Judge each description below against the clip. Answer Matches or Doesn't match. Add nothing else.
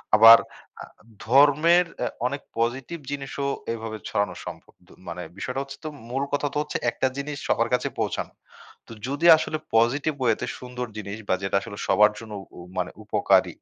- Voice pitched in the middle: Doesn't match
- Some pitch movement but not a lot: Matches